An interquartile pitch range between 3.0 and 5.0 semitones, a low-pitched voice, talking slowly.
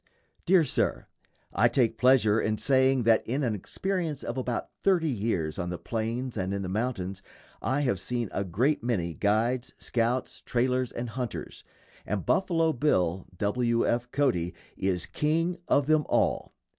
No: average, 4.6 semitones; low, 120 Hz; average, 160 wpm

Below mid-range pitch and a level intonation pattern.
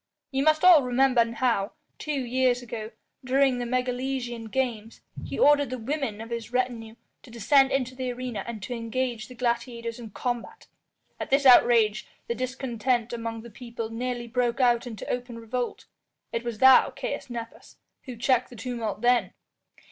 No: high, 245 Hz; narrow, 1.8 semitones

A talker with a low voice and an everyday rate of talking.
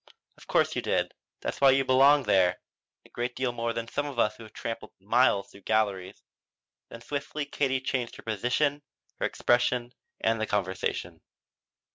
Yes: low, 120 Hz; average, 165 wpm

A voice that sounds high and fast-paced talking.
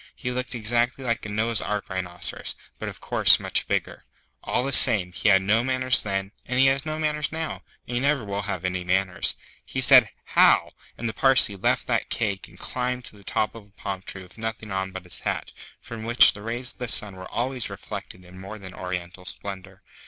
No: low, 110 Hz; fast, 220 wpm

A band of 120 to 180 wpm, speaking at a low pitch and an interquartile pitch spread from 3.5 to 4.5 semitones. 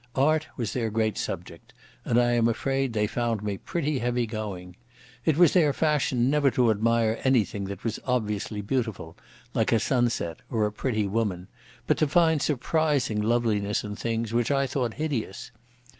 Yes: average, 170 wpm; low, 115 Hz; average, 4.1 semitones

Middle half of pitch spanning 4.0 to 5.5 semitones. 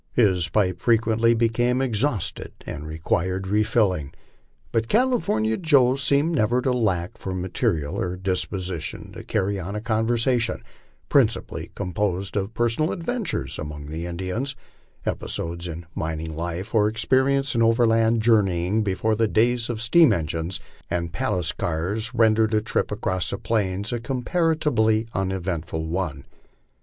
Yes: average, 4.7 semitones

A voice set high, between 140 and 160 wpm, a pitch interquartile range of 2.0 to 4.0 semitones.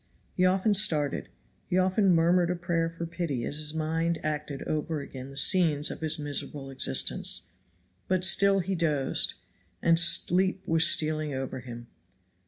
No: medium, 165 Hz; average, 155 wpm; average, 3.4 semitones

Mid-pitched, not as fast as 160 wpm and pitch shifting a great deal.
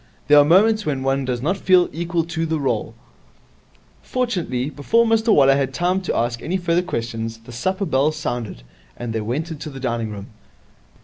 No: medium, 150 Hz; average, 185 wpm; wide, 6.4 semitones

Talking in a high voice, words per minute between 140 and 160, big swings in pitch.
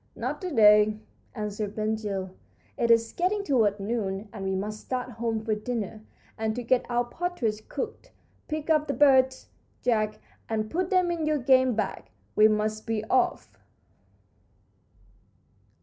No: high, 225 Hz; average, 150 wpm; average, 3.6 semitones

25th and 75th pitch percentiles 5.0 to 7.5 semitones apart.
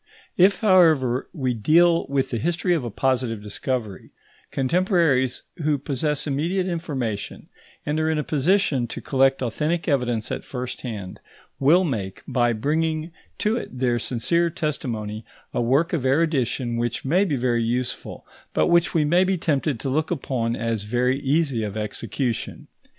Yes: average, 5.3 semitones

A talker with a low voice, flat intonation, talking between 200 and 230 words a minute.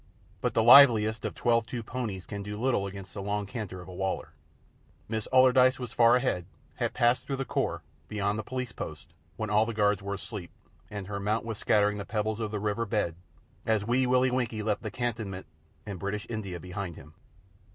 No: low, 105 Hz; average, 3.0 semitones; fast, 205 wpm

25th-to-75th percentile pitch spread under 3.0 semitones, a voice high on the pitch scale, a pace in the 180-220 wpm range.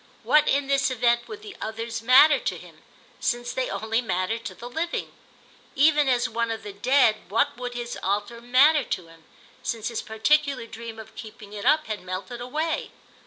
No: average, 3.7 semitones; high, 235 Hz; average, 185 wpm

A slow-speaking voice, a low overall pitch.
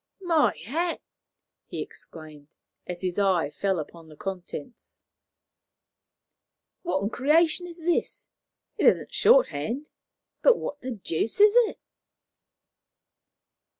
No: slow, 110 wpm; high, 220 Hz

